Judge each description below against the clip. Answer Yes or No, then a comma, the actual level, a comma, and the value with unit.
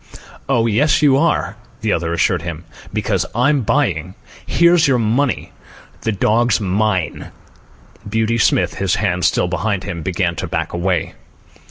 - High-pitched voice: No, low, 105 Hz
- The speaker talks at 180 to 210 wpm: No, average, 145 wpm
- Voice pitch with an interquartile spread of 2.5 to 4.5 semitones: No, average, 5.1 semitones